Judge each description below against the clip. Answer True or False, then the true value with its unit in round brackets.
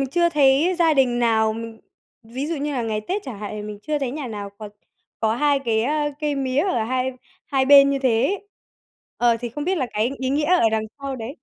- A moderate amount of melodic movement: True (4.5 semitones)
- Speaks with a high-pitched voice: True (260 Hz)